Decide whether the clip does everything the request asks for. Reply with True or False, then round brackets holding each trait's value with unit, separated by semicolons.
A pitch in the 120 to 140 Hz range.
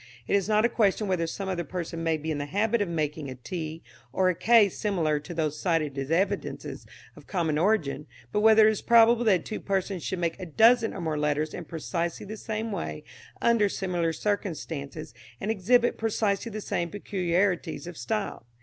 False (180 Hz)